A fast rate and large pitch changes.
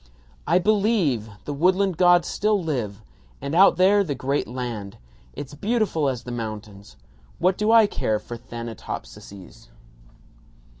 No: slow, 135 wpm; wide, 8.5 semitones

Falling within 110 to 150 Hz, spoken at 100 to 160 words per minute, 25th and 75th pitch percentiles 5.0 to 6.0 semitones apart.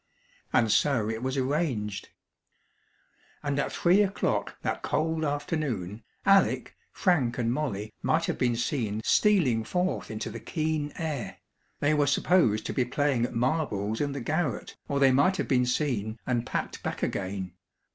Yes: low, 135 Hz; average, 155 wpm; wide, 5.4 semitones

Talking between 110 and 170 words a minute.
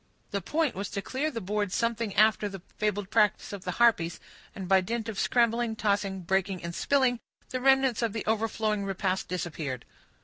No: average, 180 wpm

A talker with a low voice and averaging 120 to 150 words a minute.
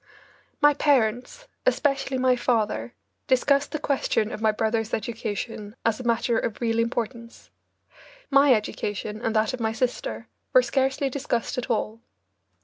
No: high, 235 Hz; average, 140 wpm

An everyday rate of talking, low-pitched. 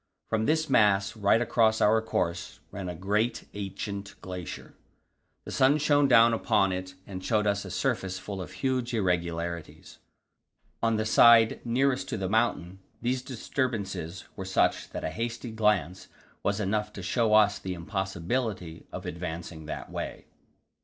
Yes: average, 155 wpm; low, 105 Hz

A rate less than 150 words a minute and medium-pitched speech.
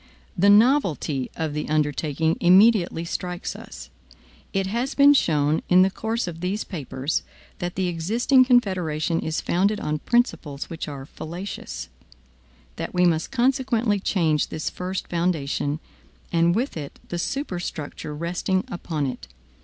Yes: average, 140 wpm; medium, 175 Hz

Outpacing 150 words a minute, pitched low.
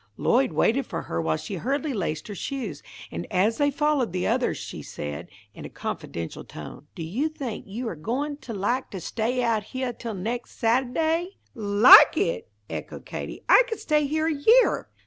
No: average, 185 wpm; high, 240 Hz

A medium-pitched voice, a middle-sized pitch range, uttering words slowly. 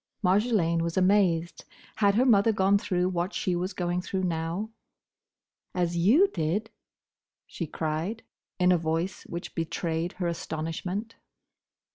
Yes: medium, 180 Hz; average, 3.2 semitones; slow, 130 wpm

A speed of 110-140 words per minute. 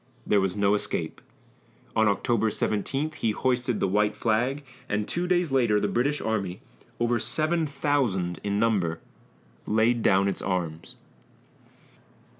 Yes: slow, 135 wpm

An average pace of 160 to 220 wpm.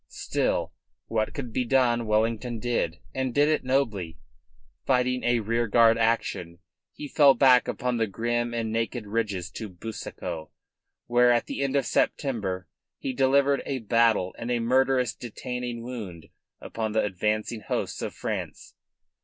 No: average, 145 wpm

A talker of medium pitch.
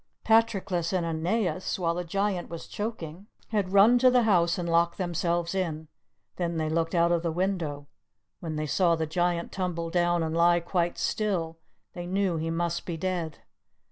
Yes: medium, 175 Hz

